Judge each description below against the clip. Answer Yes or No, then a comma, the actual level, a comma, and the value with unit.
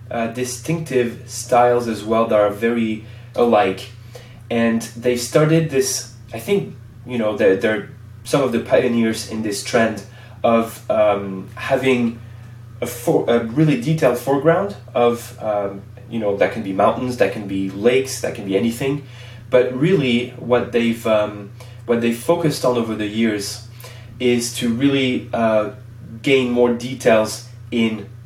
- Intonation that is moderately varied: No, narrow, 1.6 semitones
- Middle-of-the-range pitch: No, low, 120 Hz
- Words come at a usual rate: Yes, average, 150 wpm